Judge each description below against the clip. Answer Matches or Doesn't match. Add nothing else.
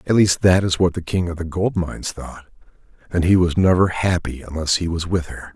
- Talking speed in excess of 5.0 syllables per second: Matches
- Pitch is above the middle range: Doesn't match